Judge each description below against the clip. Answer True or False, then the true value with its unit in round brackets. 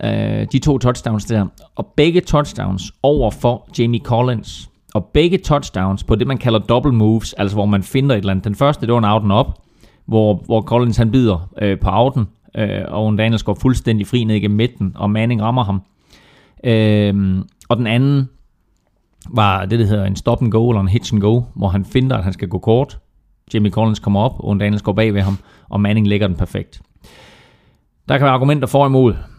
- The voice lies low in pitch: True (110 Hz)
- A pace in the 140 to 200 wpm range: False (210 wpm)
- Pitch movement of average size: True (3.4 semitones)